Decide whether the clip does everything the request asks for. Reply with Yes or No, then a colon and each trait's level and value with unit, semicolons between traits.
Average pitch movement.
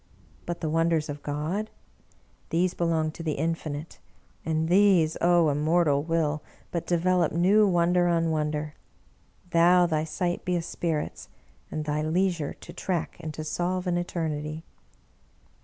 No: narrow, 2.2 semitones